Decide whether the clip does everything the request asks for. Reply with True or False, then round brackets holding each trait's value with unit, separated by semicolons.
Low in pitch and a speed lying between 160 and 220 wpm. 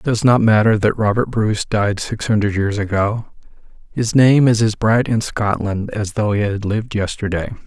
True (105 Hz; 190 wpm)